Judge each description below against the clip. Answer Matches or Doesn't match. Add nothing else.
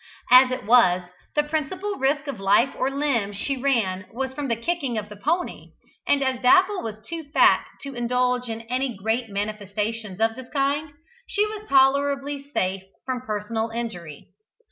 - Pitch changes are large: Doesn't match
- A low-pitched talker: Doesn't match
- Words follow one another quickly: Doesn't match